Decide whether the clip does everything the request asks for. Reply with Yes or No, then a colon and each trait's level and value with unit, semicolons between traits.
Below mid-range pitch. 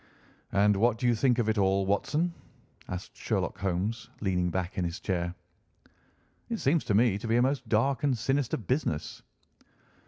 Yes: low, 110 Hz